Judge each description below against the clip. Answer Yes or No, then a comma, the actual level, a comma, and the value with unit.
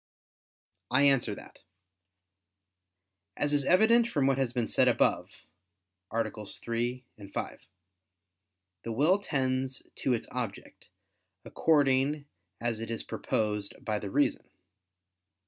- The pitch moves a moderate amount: Yes, average, 3.7 semitones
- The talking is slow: Yes, slow, 110 wpm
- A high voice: No, low, 130 Hz